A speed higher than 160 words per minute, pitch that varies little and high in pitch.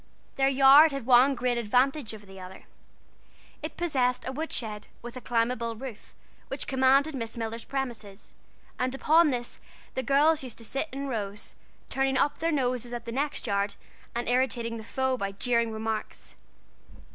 No: average, 170 wpm; average, 3.0 semitones; very high, 250 Hz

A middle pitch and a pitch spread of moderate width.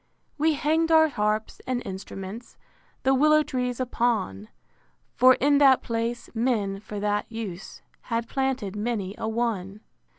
No: high, 235 Hz; average, 4.0 semitones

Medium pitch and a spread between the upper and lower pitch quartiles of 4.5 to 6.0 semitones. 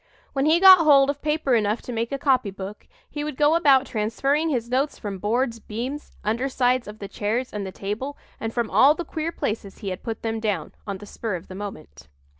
No: high, 235 Hz; average, 5.2 semitones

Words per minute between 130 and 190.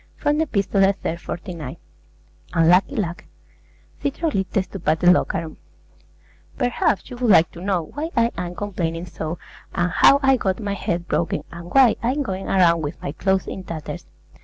Yes: average, 160 wpm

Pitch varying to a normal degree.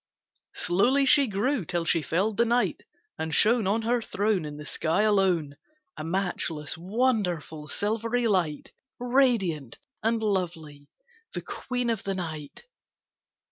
No: wide, 6.2 semitones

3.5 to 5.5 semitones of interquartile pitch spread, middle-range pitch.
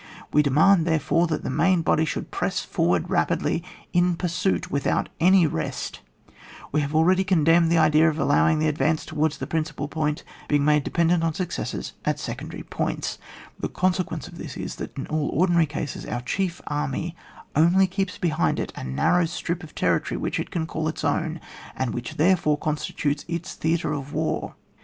No: narrow, 2.6 semitones; medium, 160 Hz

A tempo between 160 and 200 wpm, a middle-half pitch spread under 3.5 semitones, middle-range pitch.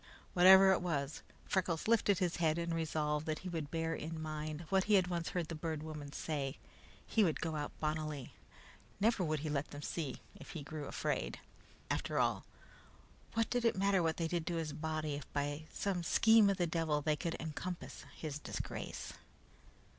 Yes: average, 190 wpm; average, 2.8 semitones; medium, 160 Hz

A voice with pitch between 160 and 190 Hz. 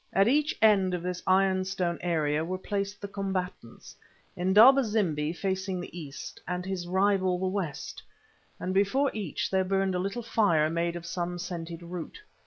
Yes: medium, 185 Hz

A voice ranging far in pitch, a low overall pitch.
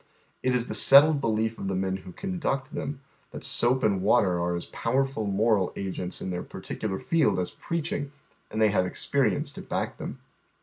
Yes: wide, 6.1 semitones; low, 110 Hz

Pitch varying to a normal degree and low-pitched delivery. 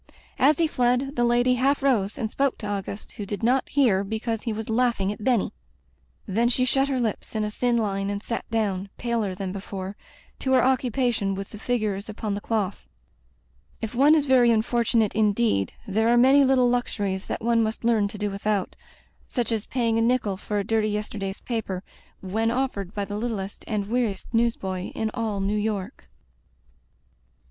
No: average, 3.2 semitones; high, 220 Hz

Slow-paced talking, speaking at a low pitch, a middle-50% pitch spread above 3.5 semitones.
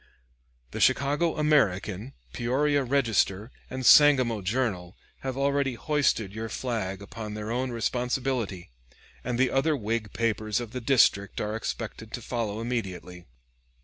Yes: slow, 130 wpm; low, 115 Hz; average, 3.9 semitones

